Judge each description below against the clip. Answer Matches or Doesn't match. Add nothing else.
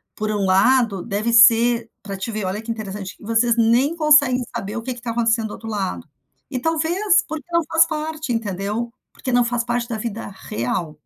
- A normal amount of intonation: Matches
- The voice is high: Matches